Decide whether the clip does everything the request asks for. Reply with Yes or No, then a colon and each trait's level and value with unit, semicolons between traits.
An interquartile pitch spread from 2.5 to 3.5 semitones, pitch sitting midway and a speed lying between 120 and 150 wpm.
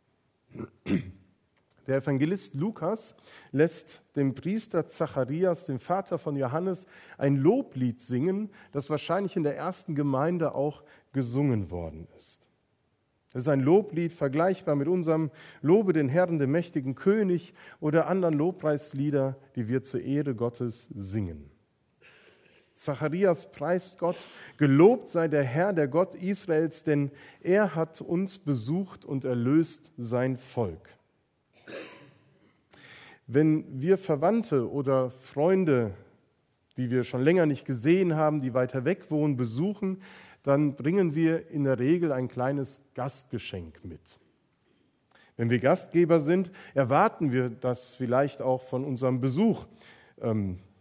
No: average, 4.8 semitones; medium, 145 Hz; slow, 125 wpm